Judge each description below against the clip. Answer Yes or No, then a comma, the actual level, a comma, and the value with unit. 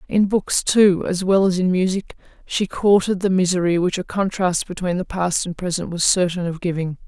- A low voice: No, medium, 185 Hz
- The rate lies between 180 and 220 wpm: Yes, fast, 205 wpm